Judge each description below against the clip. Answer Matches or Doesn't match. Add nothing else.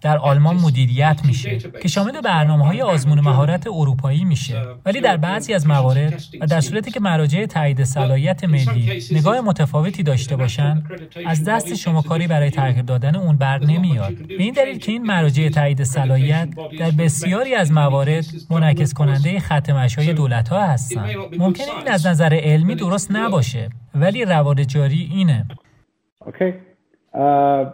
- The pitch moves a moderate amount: Matches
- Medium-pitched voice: Matches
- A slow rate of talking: Doesn't match